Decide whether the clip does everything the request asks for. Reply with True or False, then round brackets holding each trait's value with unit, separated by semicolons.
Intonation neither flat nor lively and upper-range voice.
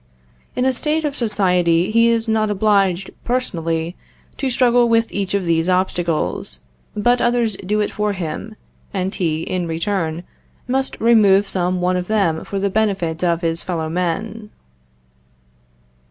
True (4.4 semitones; 195 Hz)